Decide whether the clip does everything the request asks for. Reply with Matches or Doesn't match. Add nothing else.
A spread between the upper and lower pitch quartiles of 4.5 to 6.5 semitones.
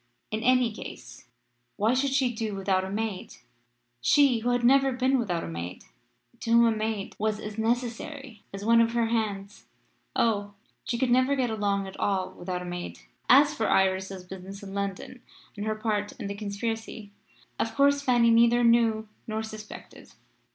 Doesn't match